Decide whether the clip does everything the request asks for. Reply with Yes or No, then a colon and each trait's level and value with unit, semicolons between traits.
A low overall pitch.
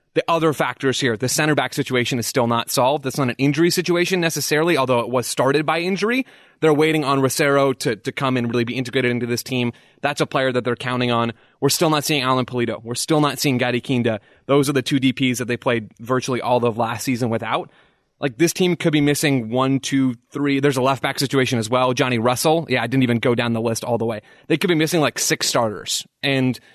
Yes: low, 130 Hz